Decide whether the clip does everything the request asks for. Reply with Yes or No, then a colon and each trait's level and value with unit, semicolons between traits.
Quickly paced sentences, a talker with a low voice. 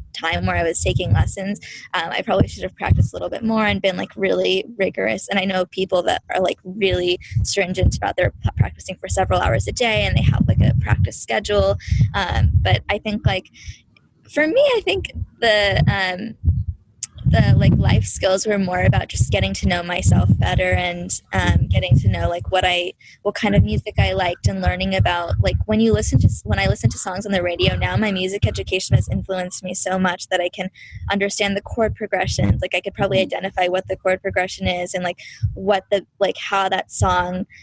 No: fast, 210 wpm; medium, 185 Hz